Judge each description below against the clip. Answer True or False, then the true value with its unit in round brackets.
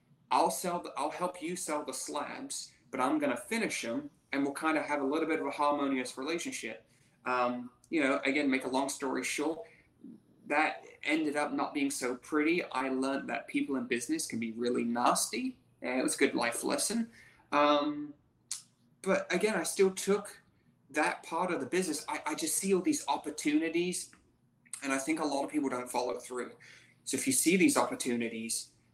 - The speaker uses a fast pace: False (195 wpm)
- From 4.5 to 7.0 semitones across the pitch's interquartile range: True (5.0 semitones)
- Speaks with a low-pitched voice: False (145 Hz)